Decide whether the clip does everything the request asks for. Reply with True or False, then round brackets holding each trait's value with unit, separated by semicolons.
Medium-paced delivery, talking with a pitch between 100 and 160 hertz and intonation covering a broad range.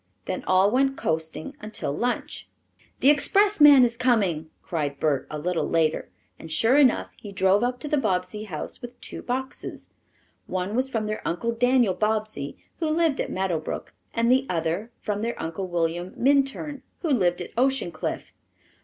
False (170 wpm; 215 Hz; 6.8 semitones)